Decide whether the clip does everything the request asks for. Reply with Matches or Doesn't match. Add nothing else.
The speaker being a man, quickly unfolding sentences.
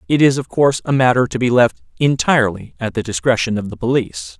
Matches